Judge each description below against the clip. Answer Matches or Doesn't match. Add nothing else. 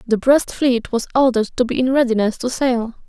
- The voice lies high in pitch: Matches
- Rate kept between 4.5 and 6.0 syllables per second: Matches